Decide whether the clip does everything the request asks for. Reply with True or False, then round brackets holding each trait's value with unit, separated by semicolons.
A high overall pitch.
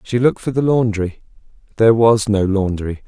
False (110 Hz)